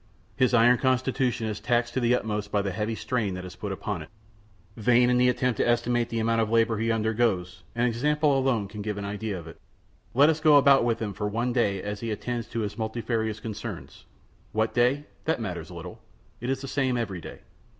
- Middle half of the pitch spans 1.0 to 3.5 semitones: Yes, average, 2.9 semitones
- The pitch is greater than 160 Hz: No, low, 115 Hz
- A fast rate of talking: Yes, fast, 220 wpm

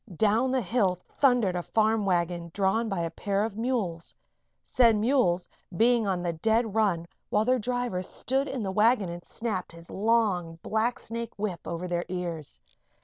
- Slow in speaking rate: No, average, 165 wpm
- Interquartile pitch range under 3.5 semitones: No, average, 4.7 semitones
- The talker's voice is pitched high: Yes, high, 210 Hz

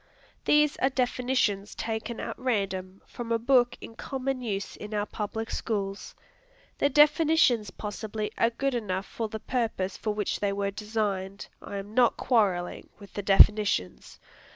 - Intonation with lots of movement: No, average, 3.6 semitones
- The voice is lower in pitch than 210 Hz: No, high, 215 Hz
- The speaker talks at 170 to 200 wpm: No, average, 155 wpm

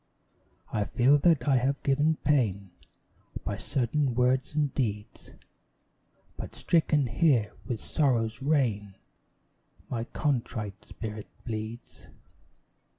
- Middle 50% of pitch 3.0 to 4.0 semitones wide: No, average, 4.5 semitones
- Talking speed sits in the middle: No, slow, 100 wpm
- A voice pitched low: Yes, low, 125 Hz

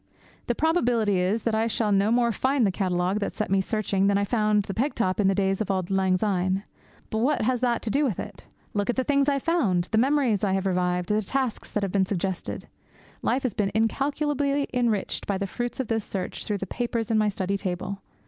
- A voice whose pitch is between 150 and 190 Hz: No, high, 210 Hz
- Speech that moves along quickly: Yes, fast, 235 wpm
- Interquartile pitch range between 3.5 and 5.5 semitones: Yes, average, 4.0 semitones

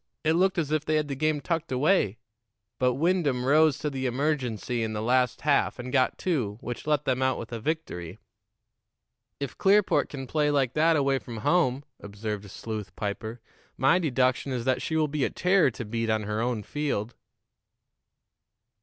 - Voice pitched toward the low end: Yes, low, 130 Hz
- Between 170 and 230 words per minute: Yes, average, 180 wpm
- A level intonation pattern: No, average, 4.7 semitones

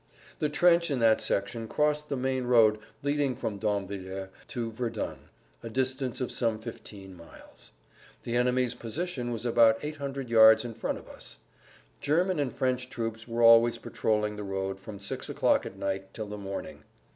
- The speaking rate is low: No, average, 170 wpm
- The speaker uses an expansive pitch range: No, average, 3.6 semitones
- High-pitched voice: No, low, 115 Hz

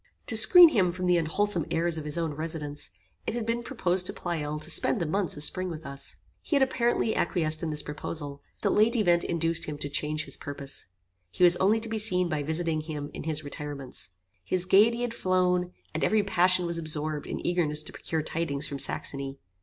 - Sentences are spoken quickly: Yes, fast, 215 wpm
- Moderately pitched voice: Yes, medium, 170 Hz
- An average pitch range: Yes, average, 3.6 semitones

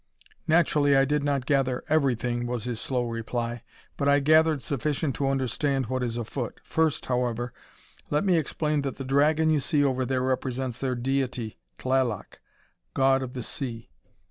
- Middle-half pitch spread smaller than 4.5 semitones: Yes, average, 2.7 semitones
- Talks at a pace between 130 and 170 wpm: Yes, average, 165 wpm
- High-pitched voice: No, low, 135 Hz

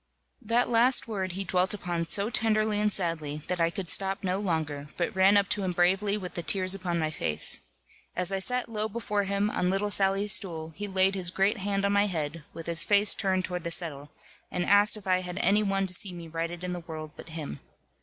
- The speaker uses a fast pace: Yes, fast, 230 wpm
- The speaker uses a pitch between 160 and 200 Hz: Yes, high, 190 Hz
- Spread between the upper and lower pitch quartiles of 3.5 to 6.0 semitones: No, average, 3.0 semitones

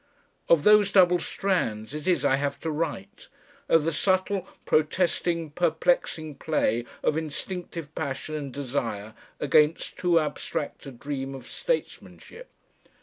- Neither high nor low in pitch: Yes, medium, 155 Hz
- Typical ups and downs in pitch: Yes, average, 3.9 semitones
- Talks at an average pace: No, slow, 130 wpm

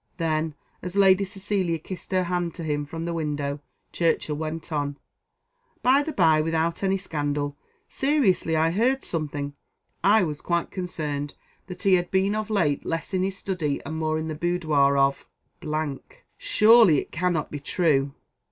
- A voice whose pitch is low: No, medium, 165 Hz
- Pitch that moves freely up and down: No, average, 4.0 semitones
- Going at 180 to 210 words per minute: No, average, 160 wpm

